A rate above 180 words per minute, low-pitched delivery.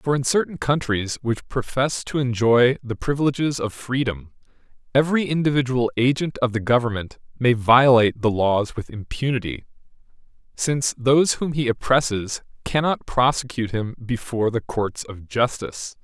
No: average, 140 wpm; low, 125 Hz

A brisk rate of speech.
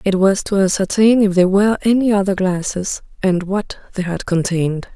No: average, 180 wpm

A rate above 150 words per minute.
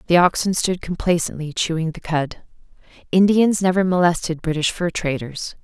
No: average, 140 wpm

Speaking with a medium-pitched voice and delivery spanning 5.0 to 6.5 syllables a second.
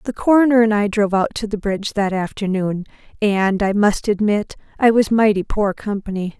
No: high, 205 Hz; 5.4 syllables/s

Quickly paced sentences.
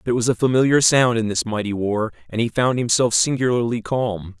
Yes: fast, 220 wpm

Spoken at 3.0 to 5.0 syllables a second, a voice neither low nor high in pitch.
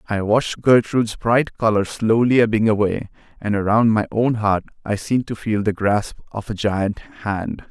No: 4.6 syllables/s; low, 110 Hz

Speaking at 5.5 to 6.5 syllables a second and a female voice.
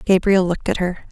No: 6.7 syllables/s; female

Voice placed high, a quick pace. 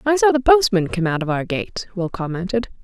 Yes: high, 210 Hz; fast, 235 wpm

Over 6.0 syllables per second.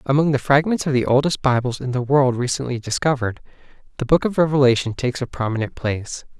Yes: 6.4 syllables/s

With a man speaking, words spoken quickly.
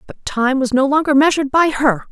No: female; fast, 225 wpm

